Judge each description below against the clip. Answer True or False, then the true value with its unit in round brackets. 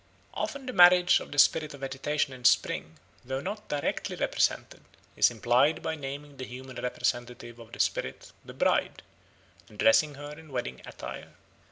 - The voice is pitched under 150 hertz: True (135 Hz)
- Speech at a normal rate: True (165 wpm)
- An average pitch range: True (3.7 semitones)